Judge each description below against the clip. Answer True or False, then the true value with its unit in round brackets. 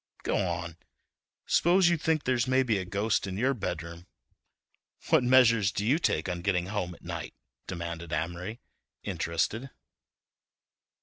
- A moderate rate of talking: False (130 wpm)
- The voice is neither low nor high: False (100 Hz)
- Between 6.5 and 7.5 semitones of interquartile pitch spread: True (6.8 semitones)